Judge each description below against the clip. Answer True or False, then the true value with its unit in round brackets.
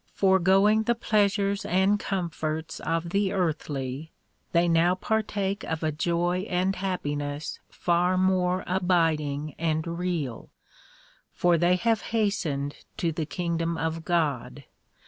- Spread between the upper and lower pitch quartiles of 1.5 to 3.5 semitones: True (3.1 semitones)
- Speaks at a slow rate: True (125 wpm)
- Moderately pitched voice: True (175 Hz)